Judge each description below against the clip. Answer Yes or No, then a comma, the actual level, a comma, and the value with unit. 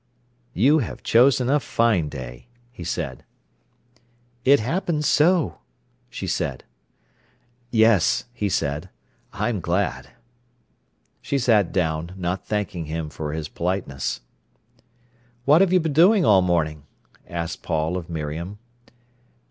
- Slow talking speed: Yes, slow, 120 wpm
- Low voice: Yes, very low, 95 Hz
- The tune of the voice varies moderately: No, wide, 8.2 semitones